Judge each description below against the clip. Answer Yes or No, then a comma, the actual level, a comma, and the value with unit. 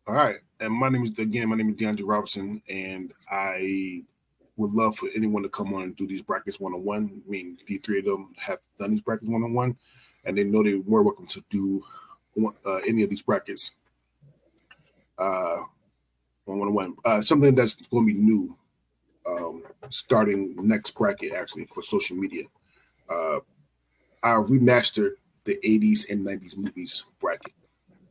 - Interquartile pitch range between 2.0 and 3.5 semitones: Yes, narrow, 2.5 semitones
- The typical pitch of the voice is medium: No, low, 105 Hz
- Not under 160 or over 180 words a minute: Yes, average, 170 wpm